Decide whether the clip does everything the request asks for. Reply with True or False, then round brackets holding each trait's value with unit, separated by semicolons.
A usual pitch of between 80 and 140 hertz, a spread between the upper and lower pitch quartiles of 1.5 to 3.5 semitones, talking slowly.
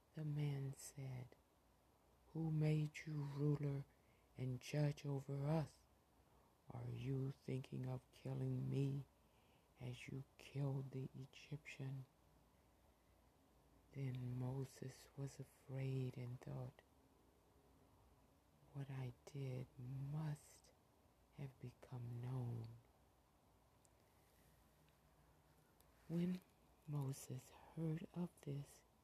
True (135 Hz; 2.4 semitones; 85 wpm)